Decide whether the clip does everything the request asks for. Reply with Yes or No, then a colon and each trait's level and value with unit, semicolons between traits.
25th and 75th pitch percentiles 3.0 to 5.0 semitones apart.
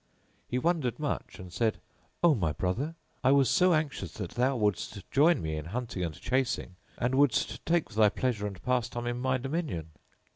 No: wide, 5.5 semitones